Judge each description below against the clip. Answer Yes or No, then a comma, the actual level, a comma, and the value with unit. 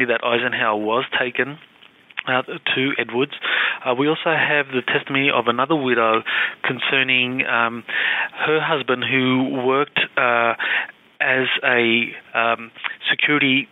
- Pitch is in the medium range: No, low, 130 Hz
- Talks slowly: Yes, slow, 120 wpm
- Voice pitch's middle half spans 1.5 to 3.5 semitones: Yes, average, 2.7 semitones